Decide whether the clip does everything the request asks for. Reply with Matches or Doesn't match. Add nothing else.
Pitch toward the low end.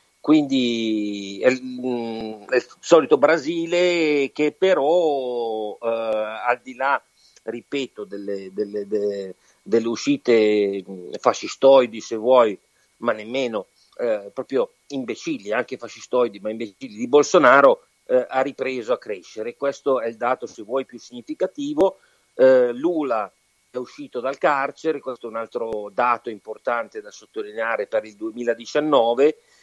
Matches